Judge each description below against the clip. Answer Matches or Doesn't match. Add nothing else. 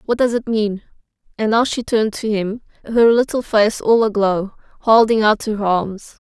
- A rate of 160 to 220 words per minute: Matches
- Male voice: Doesn't match